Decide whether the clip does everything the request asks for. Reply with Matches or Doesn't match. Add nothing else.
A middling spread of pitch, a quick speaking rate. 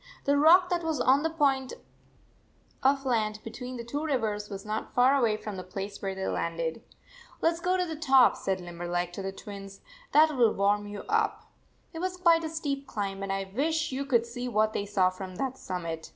Doesn't match